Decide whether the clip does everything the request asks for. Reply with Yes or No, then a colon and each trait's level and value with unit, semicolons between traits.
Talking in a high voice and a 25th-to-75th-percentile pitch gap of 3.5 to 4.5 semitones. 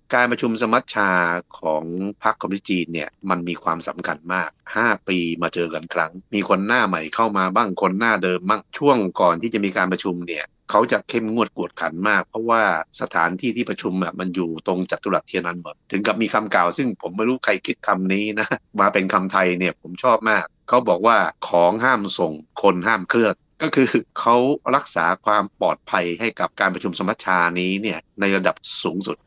No: very low, 95 Hz; average, 3.9 semitones